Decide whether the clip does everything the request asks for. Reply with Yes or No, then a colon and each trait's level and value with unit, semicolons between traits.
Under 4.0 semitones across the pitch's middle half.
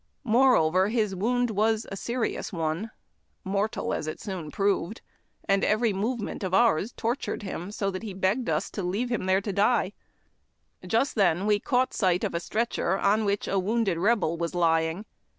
Yes: average, 3.3 semitones